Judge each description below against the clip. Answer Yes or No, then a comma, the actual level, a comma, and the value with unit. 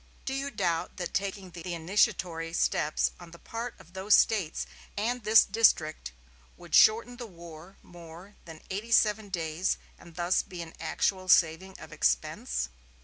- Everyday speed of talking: Yes, average, 155 wpm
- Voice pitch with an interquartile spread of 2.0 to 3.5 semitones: No, average, 4.2 semitones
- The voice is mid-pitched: Yes, medium, 180 Hz